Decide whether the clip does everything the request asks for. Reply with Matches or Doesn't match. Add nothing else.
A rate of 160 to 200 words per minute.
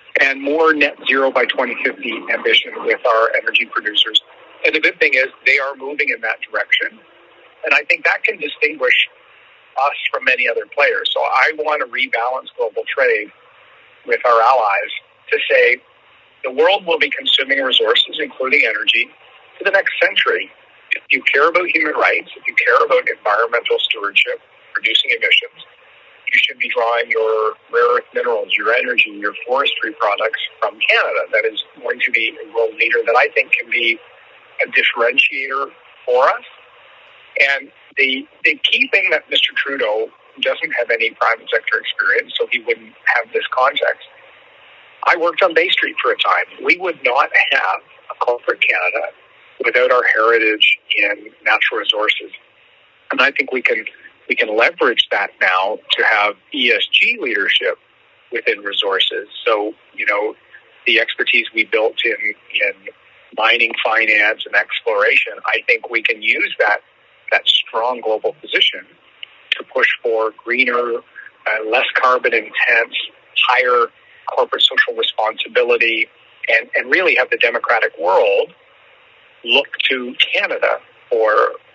Doesn't match